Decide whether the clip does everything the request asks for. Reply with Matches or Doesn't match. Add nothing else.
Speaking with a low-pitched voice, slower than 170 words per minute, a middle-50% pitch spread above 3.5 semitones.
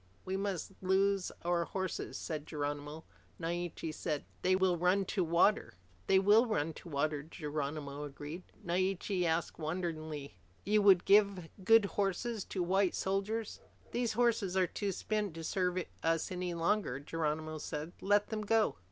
Doesn't match